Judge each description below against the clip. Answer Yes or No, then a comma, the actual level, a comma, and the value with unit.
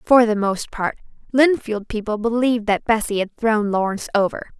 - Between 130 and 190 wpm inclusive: Yes, average, 170 wpm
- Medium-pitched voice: No, high, 220 Hz